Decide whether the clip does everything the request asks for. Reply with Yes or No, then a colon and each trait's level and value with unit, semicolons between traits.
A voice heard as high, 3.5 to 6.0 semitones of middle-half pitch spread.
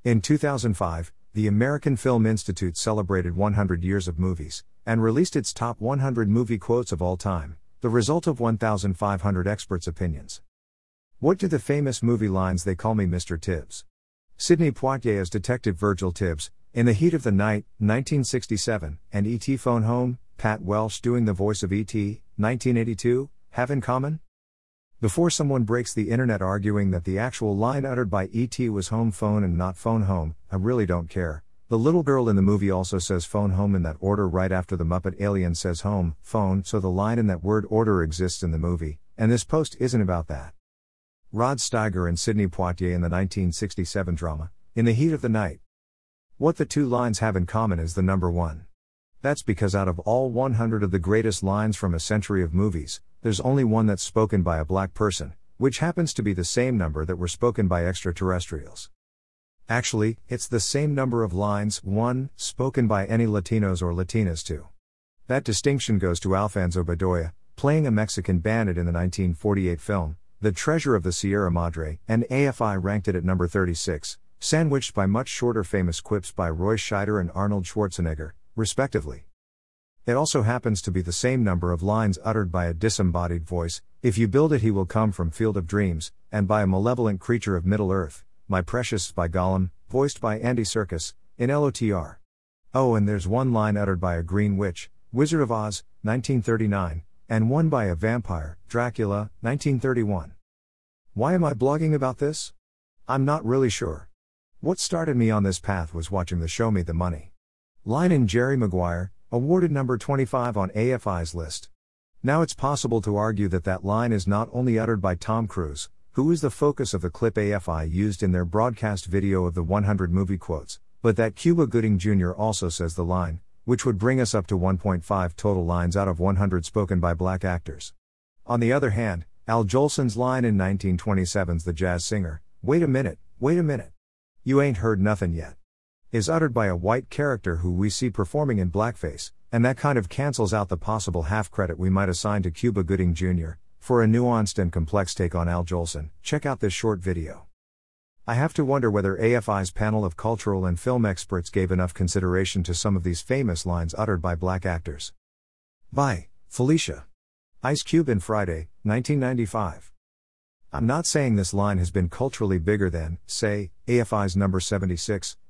No: low, 100 Hz; average, 4.7 semitones